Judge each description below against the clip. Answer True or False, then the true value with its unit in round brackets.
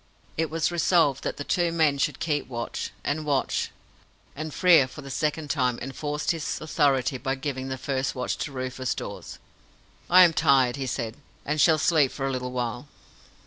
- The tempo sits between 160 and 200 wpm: True (185 wpm)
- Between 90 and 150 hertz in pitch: True (140 Hz)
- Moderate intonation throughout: True (3.1 semitones)